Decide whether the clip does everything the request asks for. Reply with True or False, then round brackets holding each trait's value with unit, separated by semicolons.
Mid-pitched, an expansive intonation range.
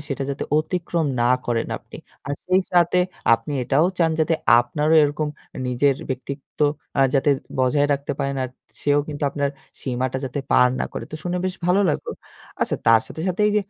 False (145 Hz; 3.7 semitones)